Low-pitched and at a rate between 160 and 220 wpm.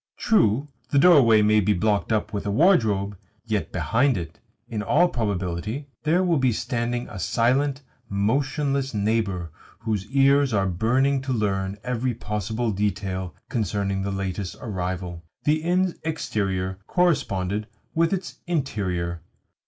No: low, 110 Hz; slow, 135 wpm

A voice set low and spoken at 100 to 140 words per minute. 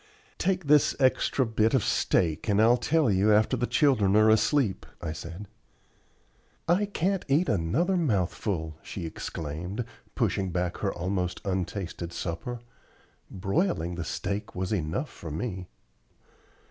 Yes: low, 100 Hz; slow, 135 wpm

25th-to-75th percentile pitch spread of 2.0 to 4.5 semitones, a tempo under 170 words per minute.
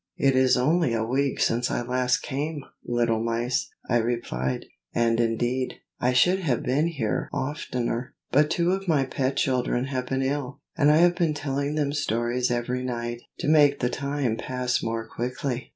No: average, 3.1 semitones; average, 175 wpm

